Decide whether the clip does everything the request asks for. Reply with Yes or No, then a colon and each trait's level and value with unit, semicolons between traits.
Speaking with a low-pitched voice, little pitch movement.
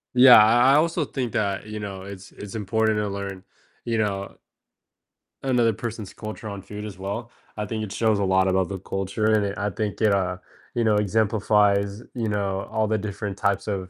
Yes: low, 105 Hz; narrow, 1.9 semitones